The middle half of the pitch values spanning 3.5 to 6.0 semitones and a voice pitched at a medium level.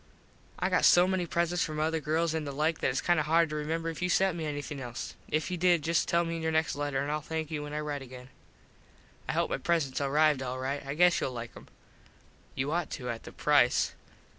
No: average, 2.8 semitones; medium, 155 Hz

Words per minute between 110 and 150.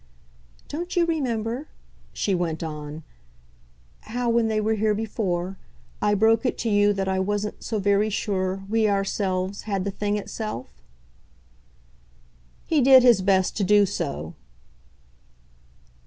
Yes: slow, 135 wpm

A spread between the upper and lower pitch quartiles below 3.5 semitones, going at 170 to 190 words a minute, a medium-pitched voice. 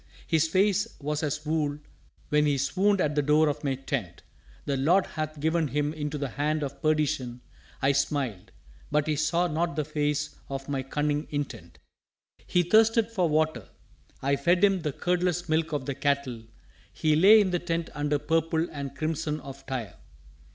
Yes: narrow, 2.6 semitones; average, 175 wpm; medium, 150 Hz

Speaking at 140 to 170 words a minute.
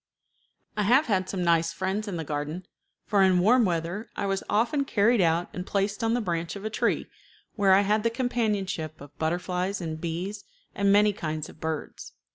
No: average, 195 wpm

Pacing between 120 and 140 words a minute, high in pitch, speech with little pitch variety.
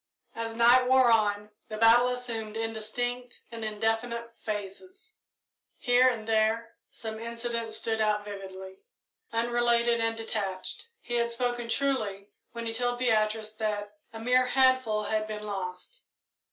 Yes: slow, 135 wpm; high, 225 Hz; narrow, 2.2 semitones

